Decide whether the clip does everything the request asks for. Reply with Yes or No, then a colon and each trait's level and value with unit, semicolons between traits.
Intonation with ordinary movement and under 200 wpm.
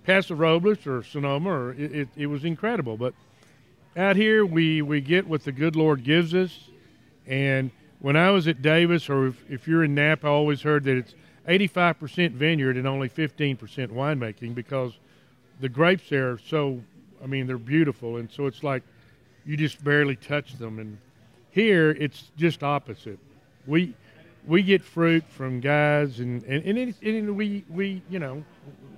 Yes: average, 4.1 semitones; average, 175 wpm